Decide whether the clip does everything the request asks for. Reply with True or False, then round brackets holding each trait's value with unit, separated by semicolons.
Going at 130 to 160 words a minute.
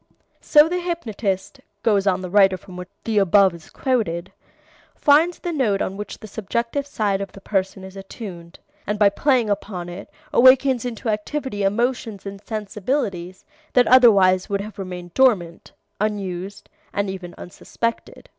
True (155 wpm)